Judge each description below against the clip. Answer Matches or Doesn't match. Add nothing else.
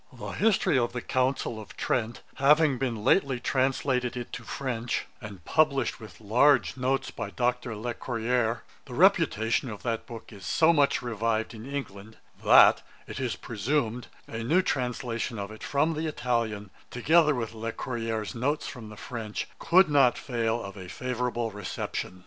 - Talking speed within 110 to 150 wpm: Doesn't match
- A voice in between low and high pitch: Doesn't match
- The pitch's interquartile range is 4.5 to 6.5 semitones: Doesn't match